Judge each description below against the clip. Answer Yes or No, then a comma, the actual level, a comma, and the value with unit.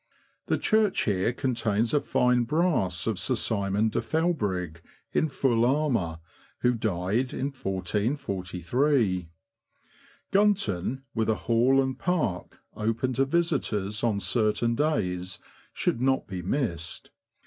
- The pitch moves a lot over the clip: Yes, wide, 5.7 semitones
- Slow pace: Yes, slow, 115 wpm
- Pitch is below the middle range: Yes, low, 115 Hz